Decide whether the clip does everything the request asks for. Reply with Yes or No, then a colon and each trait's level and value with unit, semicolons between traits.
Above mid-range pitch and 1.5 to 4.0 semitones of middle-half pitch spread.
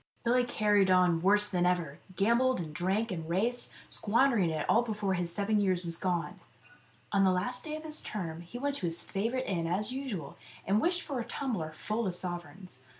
No: high, 195 Hz; average, 5.1 semitones